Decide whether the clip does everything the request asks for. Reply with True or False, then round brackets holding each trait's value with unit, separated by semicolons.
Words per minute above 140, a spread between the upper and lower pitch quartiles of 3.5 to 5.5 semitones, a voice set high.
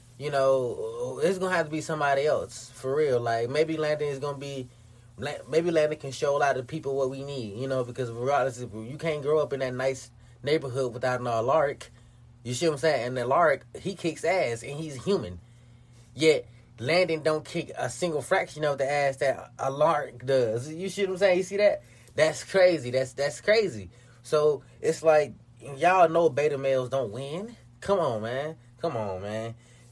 False (200 wpm; 4.5 semitones; 140 Hz)